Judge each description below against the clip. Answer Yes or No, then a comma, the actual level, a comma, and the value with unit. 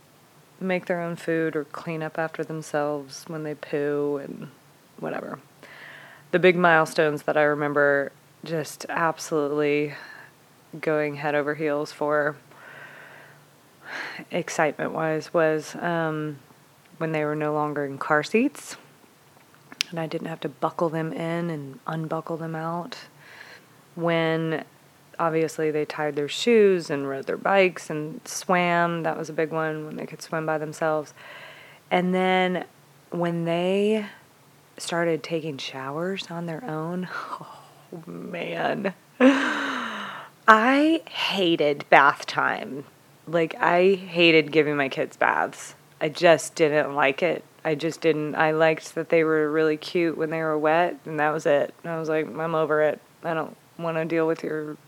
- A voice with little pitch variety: Yes, narrow, 1.9 semitones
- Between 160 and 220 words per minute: No, average, 145 wpm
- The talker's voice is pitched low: No, medium, 160 Hz